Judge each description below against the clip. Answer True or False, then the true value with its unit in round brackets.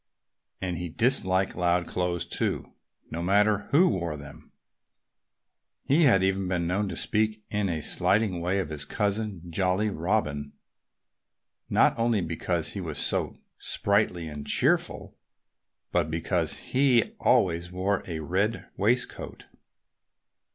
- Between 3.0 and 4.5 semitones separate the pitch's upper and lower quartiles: True (3.6 semitones)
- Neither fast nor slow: False (130 wpm)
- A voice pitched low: True (95 Hz)